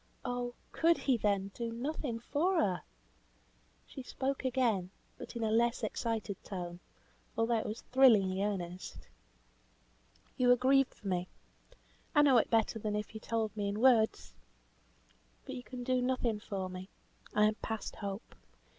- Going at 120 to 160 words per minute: Yes, average, 155 wpm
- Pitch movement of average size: Yes, average, 3.7 semitones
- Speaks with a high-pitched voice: Yes, high, 225 Hz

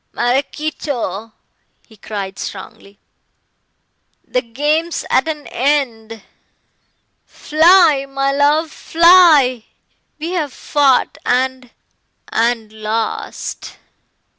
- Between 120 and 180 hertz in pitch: No, very high, 270 Hz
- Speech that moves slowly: Yes, slow, 80 wpm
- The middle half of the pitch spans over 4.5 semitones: Yes, average, 5.1 semitones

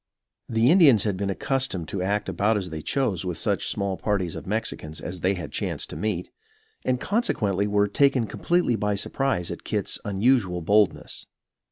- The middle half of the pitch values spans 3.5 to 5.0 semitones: Yes, average, 4.4 semitones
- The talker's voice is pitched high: No, low, 100 Hz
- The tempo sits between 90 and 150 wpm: No, average, 170 wpm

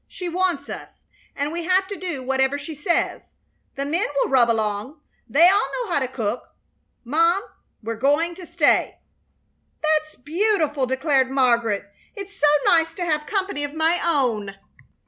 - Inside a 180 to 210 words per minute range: No, average, 165 wpm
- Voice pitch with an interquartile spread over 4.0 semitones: Yes, average, 4.7 semitones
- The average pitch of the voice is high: Yes, very high, 300 Hz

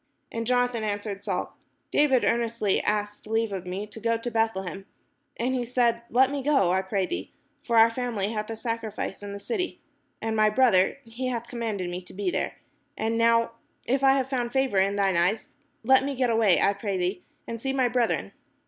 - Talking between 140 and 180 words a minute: No, fast, 205 wpm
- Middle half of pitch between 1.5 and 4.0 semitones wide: Yes, average, 3.4 semitones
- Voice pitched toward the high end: Yes, high, 225 Hz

